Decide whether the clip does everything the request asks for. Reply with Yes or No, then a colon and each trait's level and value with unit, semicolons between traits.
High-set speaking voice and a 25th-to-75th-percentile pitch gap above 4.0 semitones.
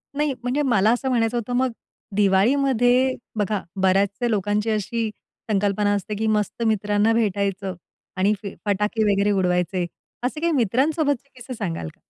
No: high, 215 Hz; average, 3.7 semitones